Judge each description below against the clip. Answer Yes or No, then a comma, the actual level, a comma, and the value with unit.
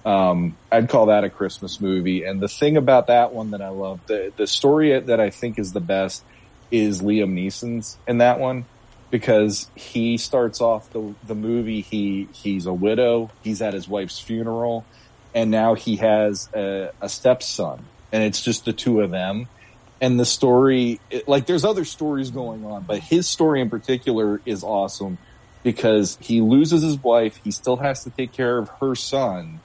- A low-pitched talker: Yes, low, 115 Hz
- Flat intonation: No, average, 3.2 semitones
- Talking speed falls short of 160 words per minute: No, average, 185 wpm